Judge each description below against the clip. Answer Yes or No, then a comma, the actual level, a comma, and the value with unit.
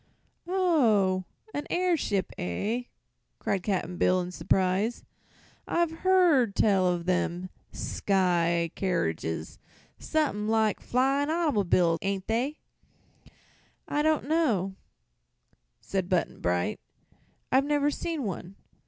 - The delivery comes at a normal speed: No, slow, 100 wpm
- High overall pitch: Yes, high, 205 Hz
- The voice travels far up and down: Yes, wide, 8.1 semitones